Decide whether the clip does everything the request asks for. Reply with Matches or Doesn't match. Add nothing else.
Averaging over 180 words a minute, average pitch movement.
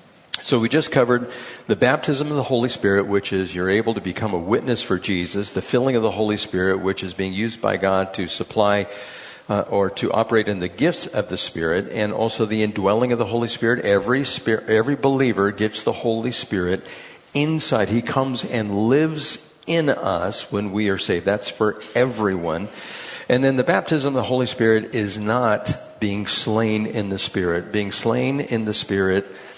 Matches